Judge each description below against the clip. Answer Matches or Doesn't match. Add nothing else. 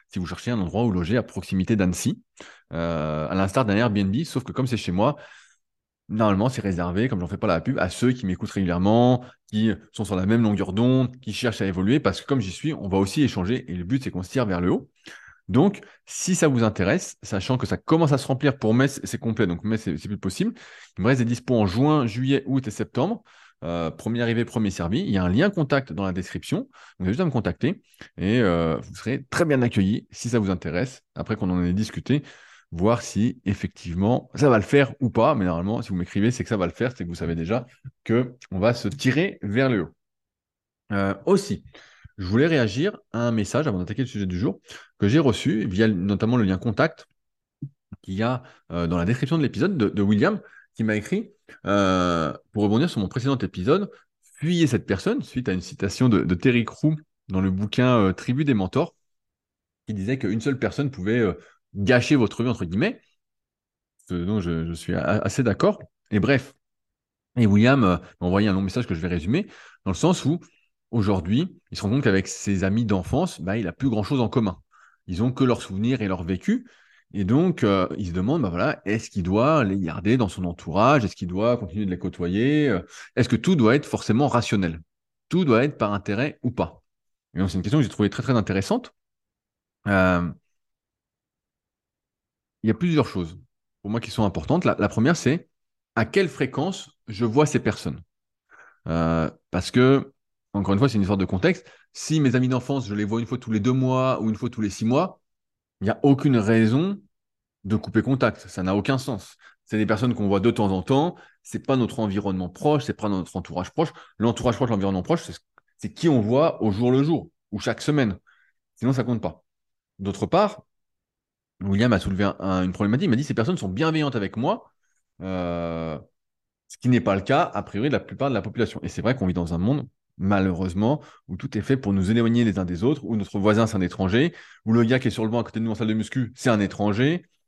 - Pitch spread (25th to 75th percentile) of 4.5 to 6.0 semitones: Matches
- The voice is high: Doesn't match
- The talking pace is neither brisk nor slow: Doesn't match